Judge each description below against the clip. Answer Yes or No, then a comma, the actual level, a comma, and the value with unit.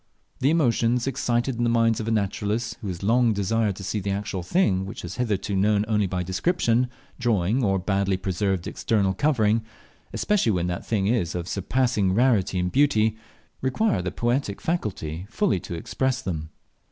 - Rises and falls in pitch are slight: No, average, 4.0 semitones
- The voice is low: Yes, low, 105 Hz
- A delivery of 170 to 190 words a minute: Yes, average, 175 wpm